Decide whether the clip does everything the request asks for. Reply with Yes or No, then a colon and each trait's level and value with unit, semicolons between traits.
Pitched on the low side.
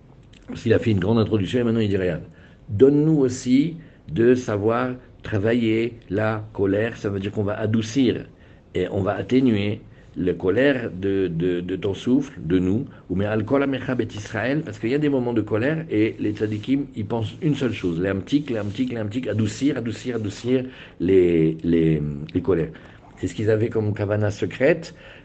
Yes: low, 110 Hz